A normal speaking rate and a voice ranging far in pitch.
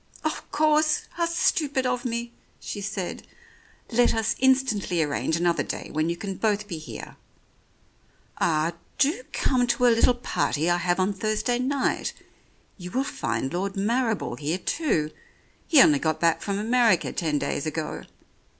Yes: average, 155 wpm; wide, 6.6 semitones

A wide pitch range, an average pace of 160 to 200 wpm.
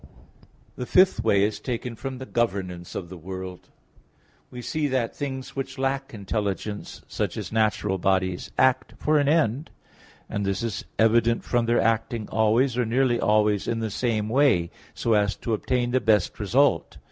No: average, 4.0 semitones; average, 170 wpm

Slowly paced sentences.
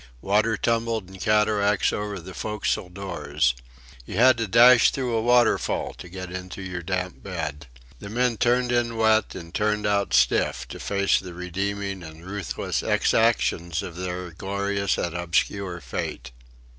No: average, 155 wpm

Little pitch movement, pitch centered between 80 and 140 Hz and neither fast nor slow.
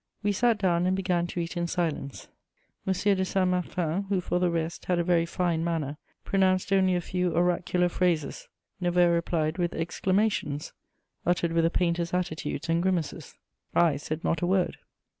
No: narrow, 1.6 semitones; medium, 175 Hz; average, 175 wpm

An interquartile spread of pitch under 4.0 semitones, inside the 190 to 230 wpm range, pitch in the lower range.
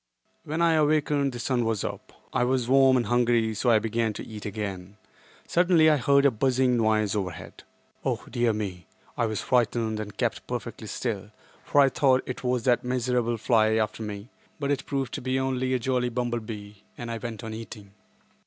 Yes: average, 3.1 semitones; average, 195 wpm; low, 120 Hz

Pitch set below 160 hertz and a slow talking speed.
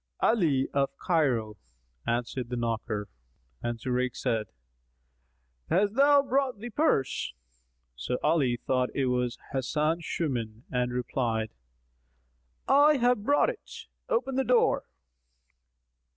Yes: low, 135 Hz; slow, 110 wpm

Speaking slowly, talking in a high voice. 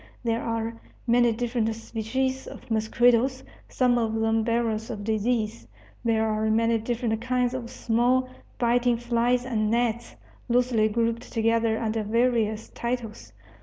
Yes: slow, 130 wpm; high, 230 Hz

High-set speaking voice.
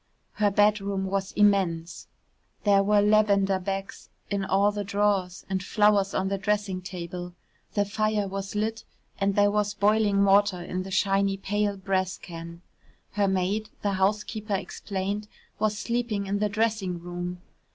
Yes: high, 200 Hz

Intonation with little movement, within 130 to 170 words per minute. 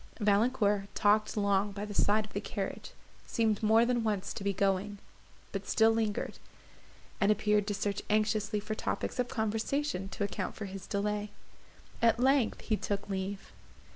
Yes: narrow, 1.6 semitones; average, 165 wpm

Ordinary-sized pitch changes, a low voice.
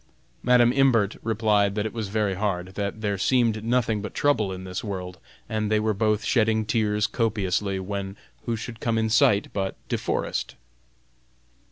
No: narrow, 2.1 semitones; low, 105 Hz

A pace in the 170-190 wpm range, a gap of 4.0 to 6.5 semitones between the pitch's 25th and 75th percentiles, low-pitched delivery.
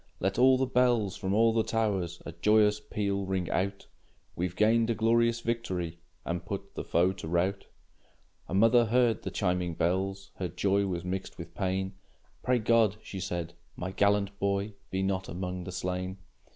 No: average, 175 wpm; average, 3.2 semitones; low, 100 Hz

